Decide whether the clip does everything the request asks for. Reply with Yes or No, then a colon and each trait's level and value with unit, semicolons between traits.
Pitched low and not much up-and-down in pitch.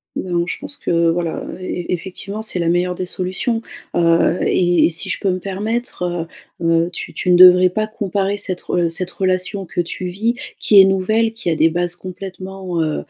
No: medium, 185 Hz; narrow, 2.0 semitones